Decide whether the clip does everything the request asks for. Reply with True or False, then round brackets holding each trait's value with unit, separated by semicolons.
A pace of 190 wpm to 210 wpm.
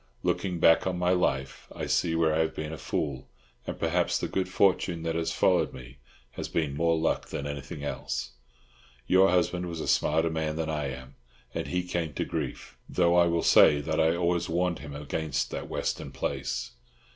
True (195 wpm)